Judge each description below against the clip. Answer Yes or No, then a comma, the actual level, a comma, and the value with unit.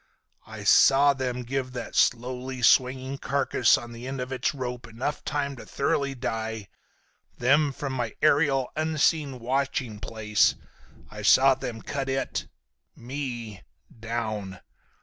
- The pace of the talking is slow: Yes, slow, 125 wpm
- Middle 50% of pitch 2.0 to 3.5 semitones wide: Yes, average, 2.8 semitones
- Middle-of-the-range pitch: No, low, 130 Hz